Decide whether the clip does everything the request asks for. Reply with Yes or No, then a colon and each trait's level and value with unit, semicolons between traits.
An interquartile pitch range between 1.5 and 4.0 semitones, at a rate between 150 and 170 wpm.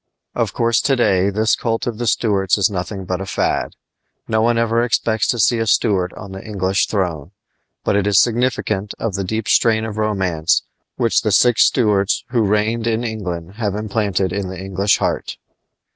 No: average, 2.8 semitones; average, 190 wpm